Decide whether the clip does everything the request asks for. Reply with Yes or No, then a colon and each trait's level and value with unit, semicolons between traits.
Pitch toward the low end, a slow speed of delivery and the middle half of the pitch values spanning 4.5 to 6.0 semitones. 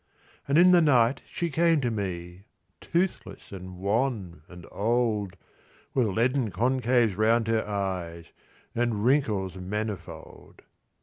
Yes: low, 110 Hz; slow, 120 wpm; average, 5.1 semitones